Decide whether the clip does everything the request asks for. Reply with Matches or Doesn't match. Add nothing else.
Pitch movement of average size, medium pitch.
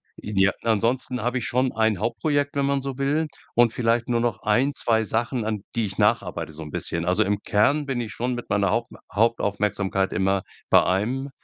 Doesn't match